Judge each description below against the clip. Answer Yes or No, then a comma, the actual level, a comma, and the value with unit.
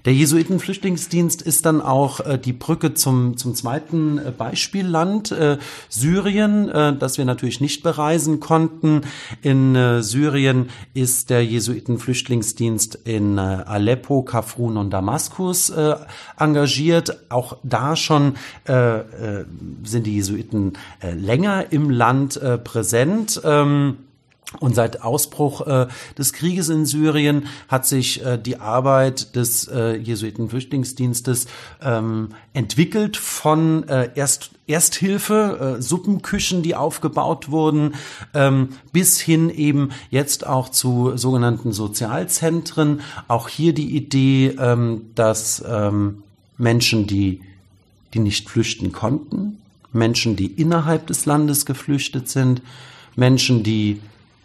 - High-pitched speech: No, low, 135 Hz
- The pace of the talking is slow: Yes, slow, 105 wpm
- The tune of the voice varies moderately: Yes, average, 4.7 semitones